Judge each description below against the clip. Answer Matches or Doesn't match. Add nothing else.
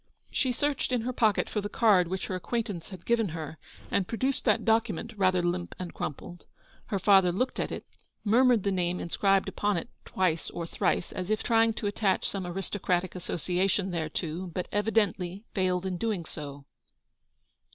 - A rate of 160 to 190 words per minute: Matches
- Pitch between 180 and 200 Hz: Matches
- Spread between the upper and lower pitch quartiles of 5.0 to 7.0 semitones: Doesn't match